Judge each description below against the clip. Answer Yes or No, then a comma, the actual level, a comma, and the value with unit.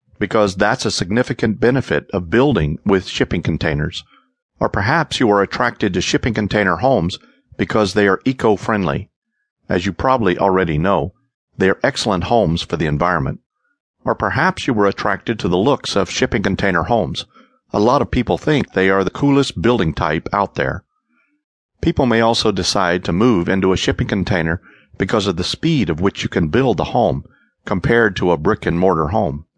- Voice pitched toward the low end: Yes, low, 100 Hz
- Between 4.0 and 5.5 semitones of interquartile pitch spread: Yes, average, 4.3 semitones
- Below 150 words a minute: No, average, 175 wpm